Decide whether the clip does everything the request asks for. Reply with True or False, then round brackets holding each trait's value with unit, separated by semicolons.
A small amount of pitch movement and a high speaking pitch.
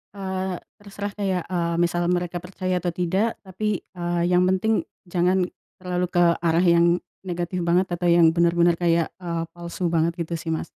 False (1.4 semitones; 175 Hz)